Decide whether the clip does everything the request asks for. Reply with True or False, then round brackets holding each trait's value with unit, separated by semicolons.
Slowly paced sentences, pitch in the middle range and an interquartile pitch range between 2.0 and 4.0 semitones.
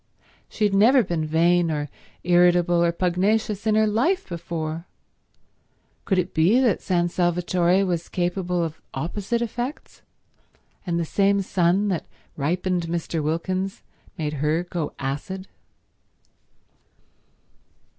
True (120 wpm; 175 Hz; 2.7 semitones)